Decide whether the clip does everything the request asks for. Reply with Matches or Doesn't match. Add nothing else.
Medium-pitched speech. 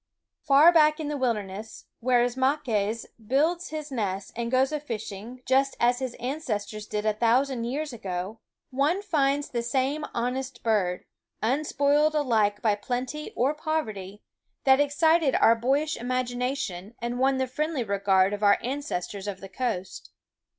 Doesn't match